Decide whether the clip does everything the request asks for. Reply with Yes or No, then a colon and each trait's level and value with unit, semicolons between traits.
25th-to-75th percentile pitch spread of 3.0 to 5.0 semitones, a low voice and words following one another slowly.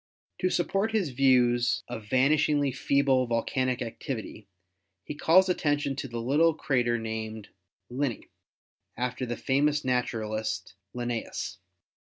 Yes: average, 3.6 semitones; low, 130 Hz; slow, 120 wpm